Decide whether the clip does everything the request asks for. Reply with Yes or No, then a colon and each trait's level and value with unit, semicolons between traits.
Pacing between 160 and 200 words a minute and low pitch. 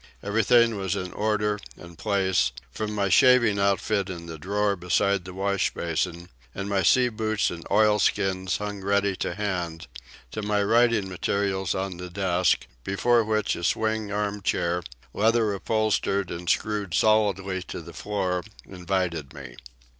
No: average, 150 wpm; low, 100 Hz